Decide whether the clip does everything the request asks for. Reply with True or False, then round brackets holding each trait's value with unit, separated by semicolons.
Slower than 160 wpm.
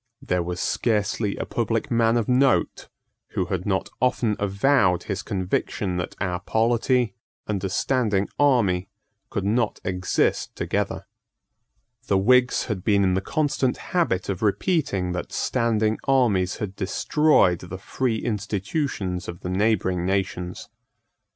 True (135 wpm)